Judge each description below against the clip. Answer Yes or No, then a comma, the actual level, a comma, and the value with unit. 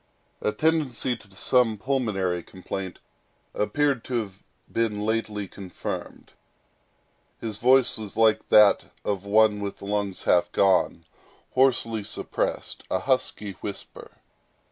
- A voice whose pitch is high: No, low, 105 Hz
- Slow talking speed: Yes, slow, 110 wpm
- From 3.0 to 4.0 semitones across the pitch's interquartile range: Yes, average, 3.3 semitones